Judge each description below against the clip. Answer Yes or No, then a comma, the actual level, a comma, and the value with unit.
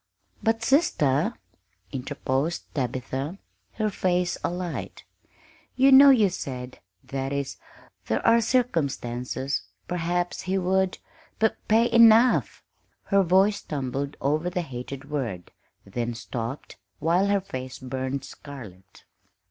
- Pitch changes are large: Yes, wide, 7.0 semitones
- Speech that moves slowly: Yes, slow, 115 wpm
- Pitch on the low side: No, medium, 155 Hz